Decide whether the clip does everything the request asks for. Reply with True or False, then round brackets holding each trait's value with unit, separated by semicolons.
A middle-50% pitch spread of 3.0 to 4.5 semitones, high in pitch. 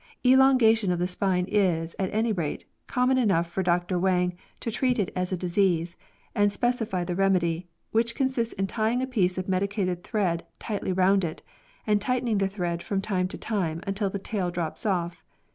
True (3.5 semitones; 195 Hz)